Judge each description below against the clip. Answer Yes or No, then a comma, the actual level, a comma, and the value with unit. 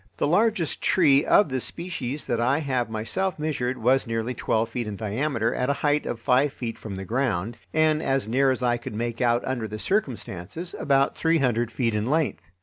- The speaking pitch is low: Yes, low, 125 Hz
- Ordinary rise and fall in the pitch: Yes, average, 4.4 semitones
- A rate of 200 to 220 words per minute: Yes, fast, 205 wpm